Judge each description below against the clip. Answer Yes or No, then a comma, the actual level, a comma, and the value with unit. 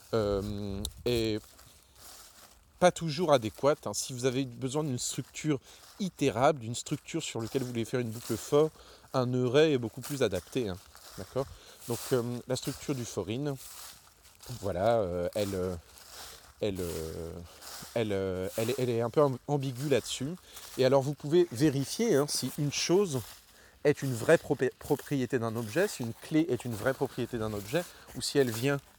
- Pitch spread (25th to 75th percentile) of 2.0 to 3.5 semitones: No, average, 5.1 semitones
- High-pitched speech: No, low, 125 Hz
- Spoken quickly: No, average, 165 wpm